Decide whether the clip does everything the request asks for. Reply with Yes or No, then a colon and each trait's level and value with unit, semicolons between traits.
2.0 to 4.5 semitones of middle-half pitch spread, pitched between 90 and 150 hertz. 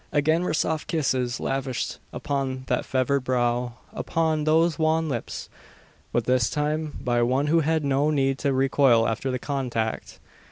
Yes: average, 3.4 semitones; low, 135 Hz